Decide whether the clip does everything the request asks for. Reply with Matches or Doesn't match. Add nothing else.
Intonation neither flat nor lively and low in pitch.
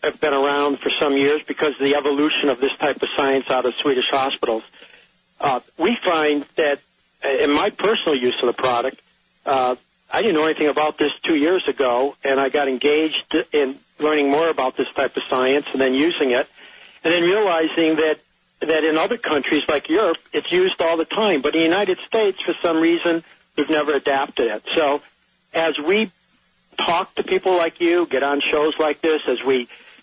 Doesn't match